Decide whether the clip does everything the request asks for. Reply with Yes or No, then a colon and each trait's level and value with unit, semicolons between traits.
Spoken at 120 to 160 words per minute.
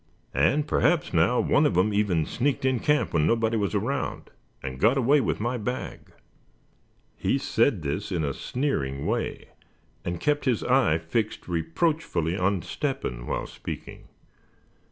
Yes: average, 155 wpm